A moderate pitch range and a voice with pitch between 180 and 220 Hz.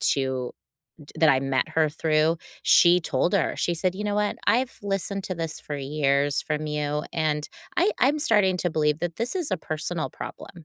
No: average, 4.1 semitones; medium, 160 Hz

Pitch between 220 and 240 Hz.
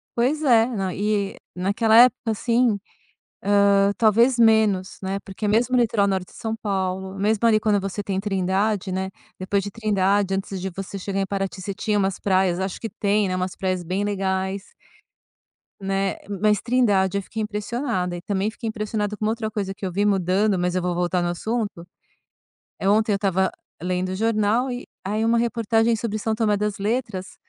No: high, 200 Hz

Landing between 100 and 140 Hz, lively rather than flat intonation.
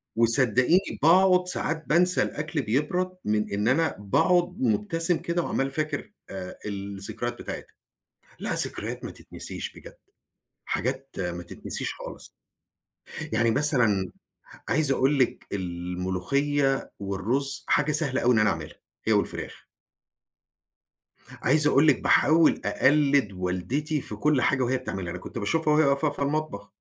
Yes: low, 135 Hz; wide, 7.0 semitones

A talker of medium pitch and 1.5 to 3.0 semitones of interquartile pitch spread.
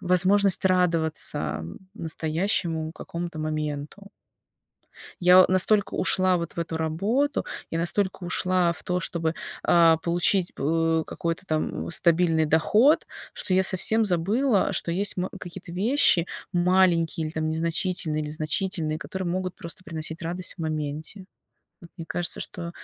Yes: medium, 170 Hz; narrow, 2.5 semitones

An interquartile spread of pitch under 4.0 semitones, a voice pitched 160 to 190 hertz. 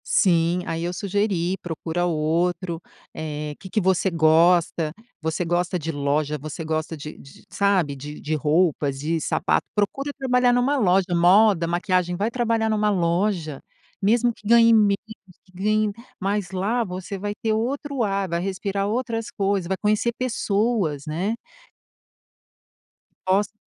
No: average, 4.3 semitones; medium, 185 Hz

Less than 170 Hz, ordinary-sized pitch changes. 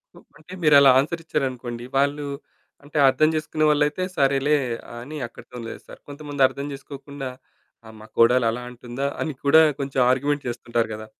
Yes: medium, 140 Hz; average, 3.0 semitones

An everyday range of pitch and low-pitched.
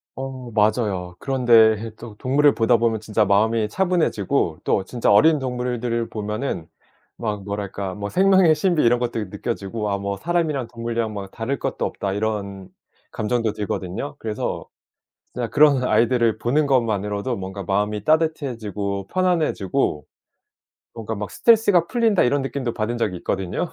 Yes: average, 4.7 semitones; low, 115 Hz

